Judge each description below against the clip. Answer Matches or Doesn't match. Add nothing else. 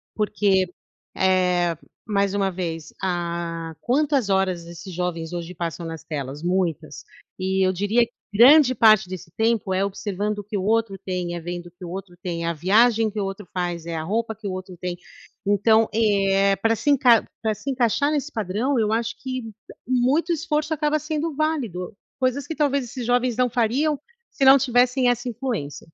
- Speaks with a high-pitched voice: Matches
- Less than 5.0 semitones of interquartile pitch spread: Doesn't match